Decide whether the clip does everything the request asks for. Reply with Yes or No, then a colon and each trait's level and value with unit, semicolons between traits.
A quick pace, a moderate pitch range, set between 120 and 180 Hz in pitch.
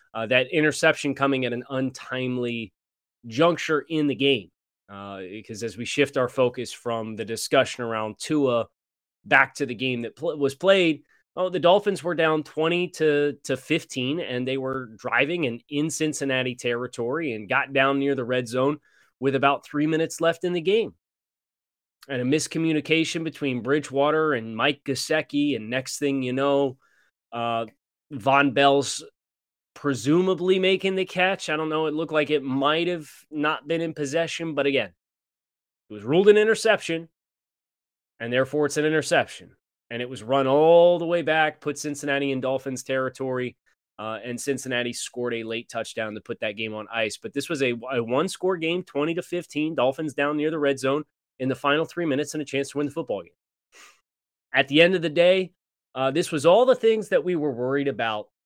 No: average, 185 wpm; average, 4.2 semitones; medium, 140 Hz